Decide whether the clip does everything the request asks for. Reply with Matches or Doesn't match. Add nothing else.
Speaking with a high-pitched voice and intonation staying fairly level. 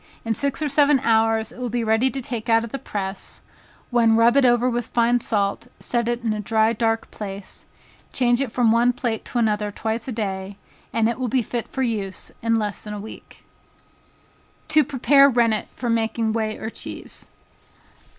Matches